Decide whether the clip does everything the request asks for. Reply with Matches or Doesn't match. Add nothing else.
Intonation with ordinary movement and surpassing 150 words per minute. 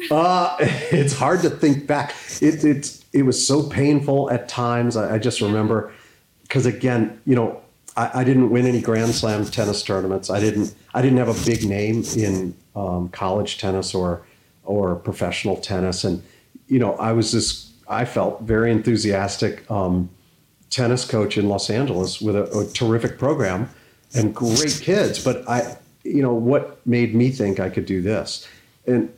Matches